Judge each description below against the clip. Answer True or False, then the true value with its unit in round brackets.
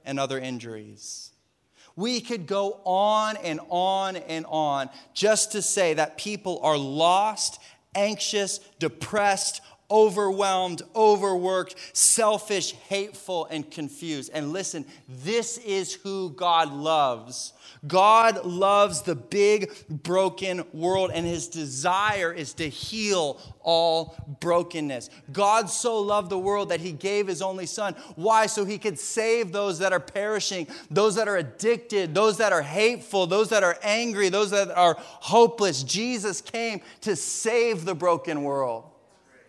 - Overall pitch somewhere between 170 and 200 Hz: True (190 Hz)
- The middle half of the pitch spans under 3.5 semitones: False (4.3 semitones)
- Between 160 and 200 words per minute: False (135 wpm)